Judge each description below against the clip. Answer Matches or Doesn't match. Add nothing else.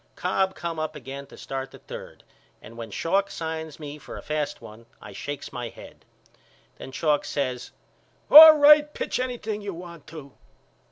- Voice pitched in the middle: Matches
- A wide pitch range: Matches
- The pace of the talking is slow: Doesn't match